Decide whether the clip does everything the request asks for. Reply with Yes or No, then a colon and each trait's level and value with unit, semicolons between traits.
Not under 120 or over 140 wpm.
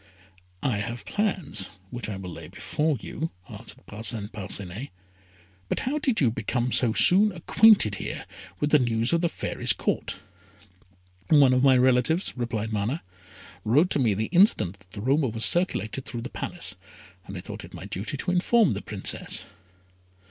No: average, 170 wpm